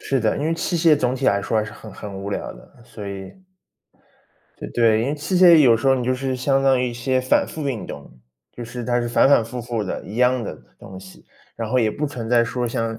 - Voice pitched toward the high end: No, low, 120 Hz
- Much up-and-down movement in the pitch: No, average, 3.1 semitones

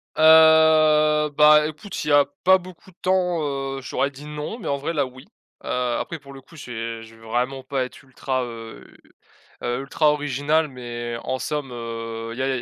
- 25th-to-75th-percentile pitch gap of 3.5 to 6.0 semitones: Yes, average, 3.9 semitones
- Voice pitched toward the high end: No, medium, 140 Hz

